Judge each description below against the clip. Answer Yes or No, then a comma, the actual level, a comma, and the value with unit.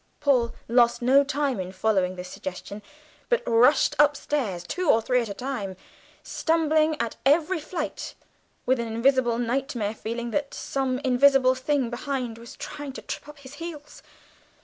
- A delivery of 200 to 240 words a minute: No, average, 160 wpm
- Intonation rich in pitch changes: No, average, 3.9 semitones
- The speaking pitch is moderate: No, very high, 255 Hz